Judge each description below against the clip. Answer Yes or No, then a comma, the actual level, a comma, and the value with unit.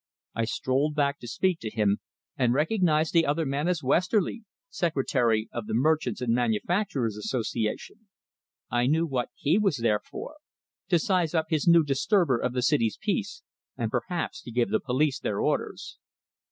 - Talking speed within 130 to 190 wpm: Yes, average, 165 wpm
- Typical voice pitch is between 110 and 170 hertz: Yes, medium, 140 Hz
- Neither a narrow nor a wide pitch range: No, wide, 5.9 semitones